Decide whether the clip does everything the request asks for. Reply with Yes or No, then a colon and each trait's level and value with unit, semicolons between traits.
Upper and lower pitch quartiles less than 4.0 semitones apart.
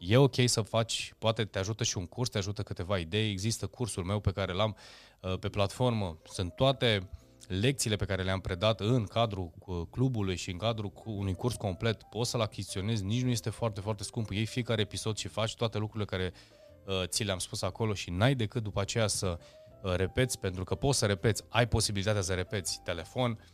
Yes: average, 3.2 semitones